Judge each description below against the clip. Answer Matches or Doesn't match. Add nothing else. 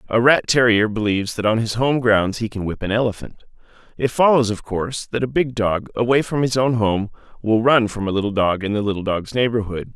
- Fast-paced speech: Matches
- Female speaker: Doesn't match